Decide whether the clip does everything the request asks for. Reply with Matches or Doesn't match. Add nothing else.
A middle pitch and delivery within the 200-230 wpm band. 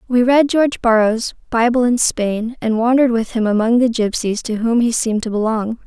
Doesn't match